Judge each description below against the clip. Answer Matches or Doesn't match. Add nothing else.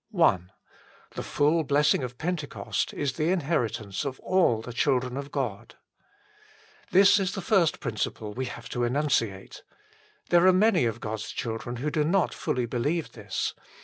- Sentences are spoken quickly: Doesn't match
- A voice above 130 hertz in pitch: Matches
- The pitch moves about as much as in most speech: Doesn't match